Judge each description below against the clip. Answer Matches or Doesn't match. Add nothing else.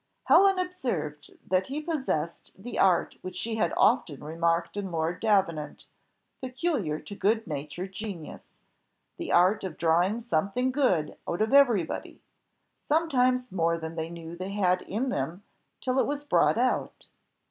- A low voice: Doesn't match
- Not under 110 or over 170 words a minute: Matches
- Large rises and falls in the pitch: Matches